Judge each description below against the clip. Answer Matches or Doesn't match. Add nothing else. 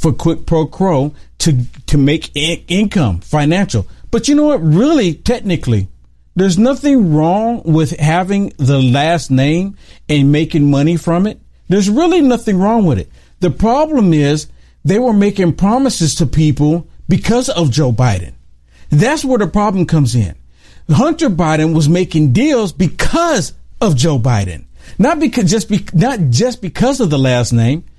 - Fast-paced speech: Doesn't match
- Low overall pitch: Doesn't match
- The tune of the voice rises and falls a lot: Matches